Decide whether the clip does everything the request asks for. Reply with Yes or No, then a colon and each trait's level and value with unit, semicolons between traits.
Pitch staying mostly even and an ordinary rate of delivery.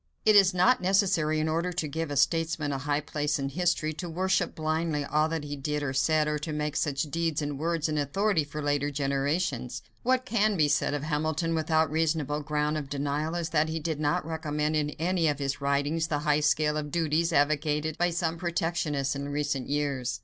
No: narrow, 2.1 semitones; fast, 210 wpm